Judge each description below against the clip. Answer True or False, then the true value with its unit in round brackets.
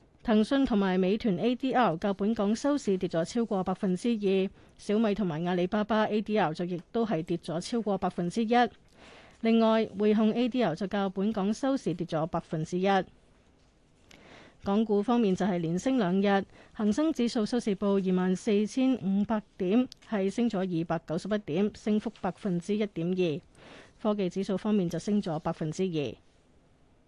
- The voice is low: False (200 Hz)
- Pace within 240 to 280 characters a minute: True (260 characters per minute)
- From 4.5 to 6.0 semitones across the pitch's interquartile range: False (3.4 semitones)